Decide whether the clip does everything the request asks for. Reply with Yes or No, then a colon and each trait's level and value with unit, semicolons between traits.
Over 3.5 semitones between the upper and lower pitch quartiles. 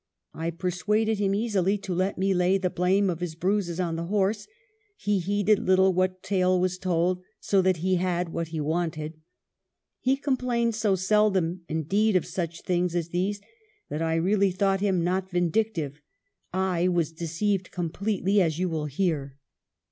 No: average, 2.8 semitones